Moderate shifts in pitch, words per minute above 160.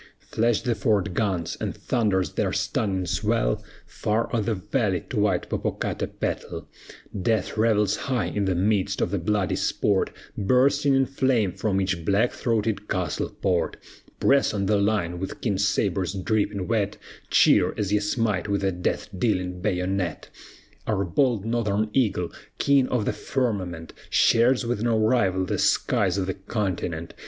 No: average, 3.3 semitones; average, 155 wpm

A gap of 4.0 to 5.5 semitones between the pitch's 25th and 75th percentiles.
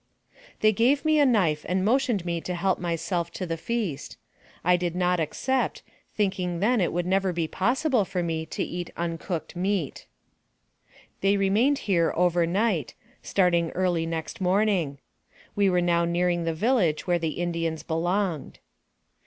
No: average, 3.1 semitones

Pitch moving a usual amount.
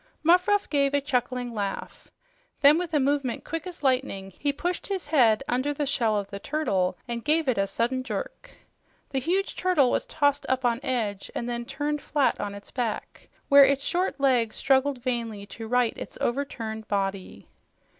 Yes: average, 4.2 semitones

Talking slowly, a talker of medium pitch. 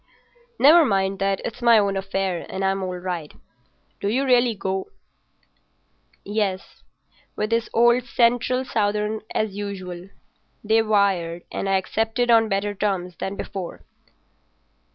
No: slow, 130 wpm; high, 200 Hz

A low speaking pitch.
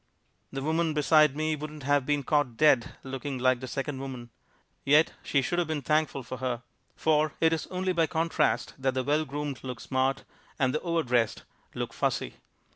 No: medium, 145 Hz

